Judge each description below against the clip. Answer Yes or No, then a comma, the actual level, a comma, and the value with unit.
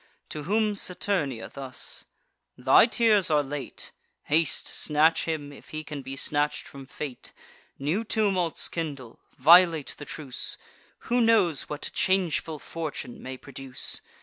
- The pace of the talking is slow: Yes, slow, 130 wpm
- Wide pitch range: No, average, 4.6 semitones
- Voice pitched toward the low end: No, medium, 155 Hz